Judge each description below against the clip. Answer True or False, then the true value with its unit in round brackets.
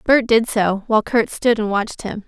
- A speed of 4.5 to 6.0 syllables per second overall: True (5.2 syllables/s)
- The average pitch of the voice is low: False (220 Hz)